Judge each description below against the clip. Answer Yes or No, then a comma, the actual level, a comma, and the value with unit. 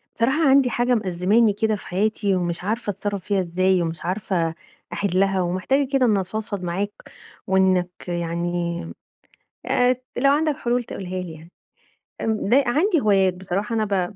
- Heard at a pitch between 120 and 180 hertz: No, high, 195 Hz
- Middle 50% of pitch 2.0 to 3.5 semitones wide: No, average, 4.3 semitones